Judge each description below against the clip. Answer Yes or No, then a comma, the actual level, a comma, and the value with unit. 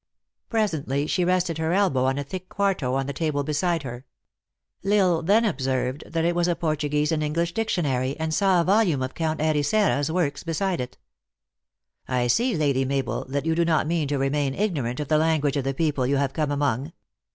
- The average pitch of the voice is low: No, medium, 155 Hz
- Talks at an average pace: No, fast, 215 wpm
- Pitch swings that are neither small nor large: Yes, average, 4.0 semitones